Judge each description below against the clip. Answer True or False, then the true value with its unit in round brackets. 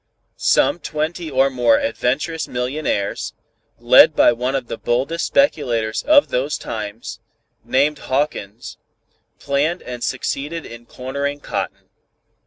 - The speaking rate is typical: False (115 wpm)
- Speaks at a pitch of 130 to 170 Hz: True (135 Hz)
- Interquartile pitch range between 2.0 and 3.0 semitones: False (4.1 semitones)